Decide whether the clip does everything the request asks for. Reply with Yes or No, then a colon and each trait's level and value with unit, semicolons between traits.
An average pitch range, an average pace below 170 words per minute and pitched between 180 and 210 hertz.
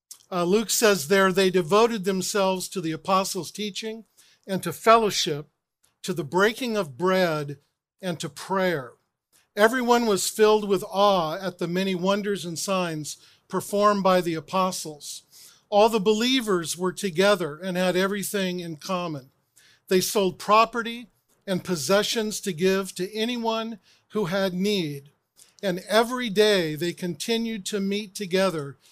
Yes: average, 3.0 semitones; average, 140 wpm; high, 190 Hz